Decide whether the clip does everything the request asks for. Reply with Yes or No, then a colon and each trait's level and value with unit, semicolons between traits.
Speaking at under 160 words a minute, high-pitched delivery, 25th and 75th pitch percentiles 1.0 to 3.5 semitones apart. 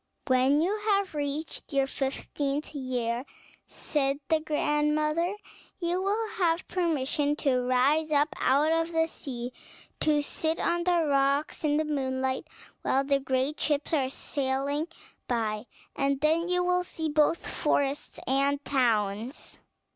Yes: average, 140 wpm; very high, 290 Hz; average, 3.1 semitones